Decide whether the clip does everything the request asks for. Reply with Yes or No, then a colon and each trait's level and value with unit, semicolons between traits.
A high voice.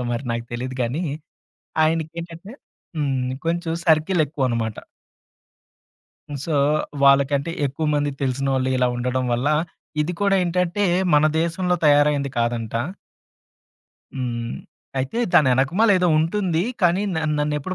No: medium, 150 Hz